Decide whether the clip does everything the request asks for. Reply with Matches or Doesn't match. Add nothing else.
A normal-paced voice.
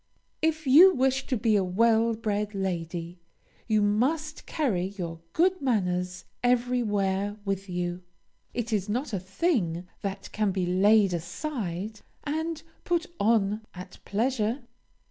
Doesn't match